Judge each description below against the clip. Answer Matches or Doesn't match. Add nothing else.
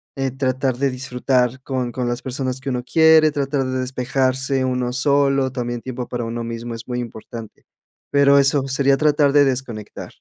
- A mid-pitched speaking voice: Doesn't match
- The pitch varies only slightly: Matches